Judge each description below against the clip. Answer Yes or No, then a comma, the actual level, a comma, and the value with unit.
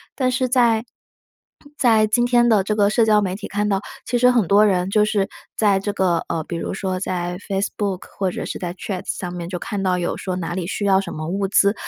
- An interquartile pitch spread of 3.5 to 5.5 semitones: No, average, 2.8 semitones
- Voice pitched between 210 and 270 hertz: No, high, 200 Hz